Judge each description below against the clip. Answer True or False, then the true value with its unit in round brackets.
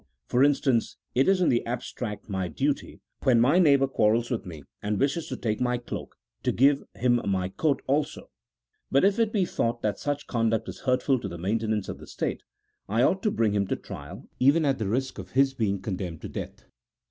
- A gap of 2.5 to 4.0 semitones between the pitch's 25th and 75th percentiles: False (4.7 semitones)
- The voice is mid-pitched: False (120 Hz)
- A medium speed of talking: False (210 wpm)